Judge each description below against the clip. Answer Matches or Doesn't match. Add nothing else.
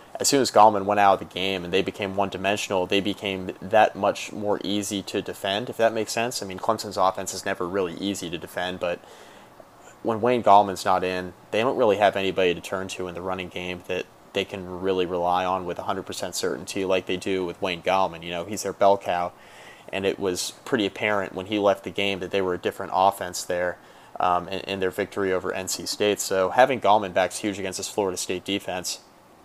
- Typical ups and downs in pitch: Doesn't match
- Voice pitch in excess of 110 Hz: Doesn't match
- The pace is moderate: Doesn't match